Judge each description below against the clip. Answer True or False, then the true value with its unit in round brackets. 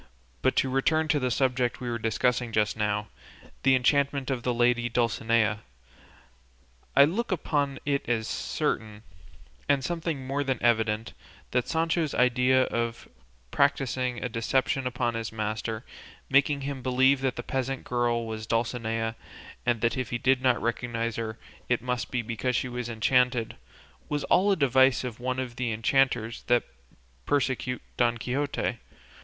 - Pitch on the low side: True (125 Hz)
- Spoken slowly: False (155 wpm)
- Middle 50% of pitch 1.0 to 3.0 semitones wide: True (2.5 semitones)